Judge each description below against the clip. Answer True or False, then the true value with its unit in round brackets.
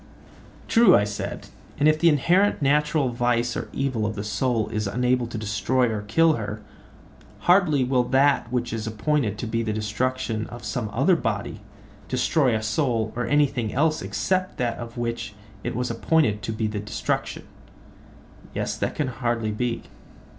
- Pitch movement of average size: True (4.3 semitones)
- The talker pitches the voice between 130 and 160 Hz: False (120 Hz)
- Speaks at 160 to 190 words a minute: True (165 wpm)